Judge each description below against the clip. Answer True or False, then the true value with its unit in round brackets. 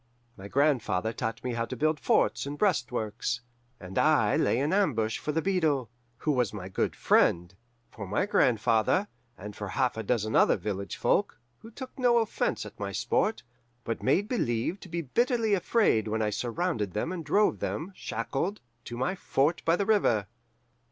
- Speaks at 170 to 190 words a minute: True (180 wpm)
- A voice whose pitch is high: False (130 Hz)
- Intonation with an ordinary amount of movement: False (8.7 semitones)